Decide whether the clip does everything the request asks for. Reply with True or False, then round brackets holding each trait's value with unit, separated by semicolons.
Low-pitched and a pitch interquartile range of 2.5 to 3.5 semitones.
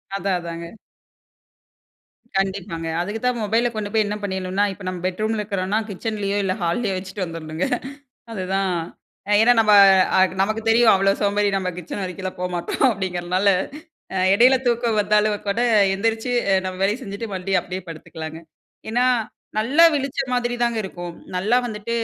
False (200 Hz; 3.2 semitones)